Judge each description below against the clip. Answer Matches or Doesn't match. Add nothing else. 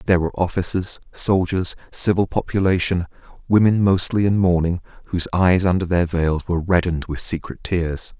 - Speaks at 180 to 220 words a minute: Doesn't match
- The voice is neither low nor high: Doesn't match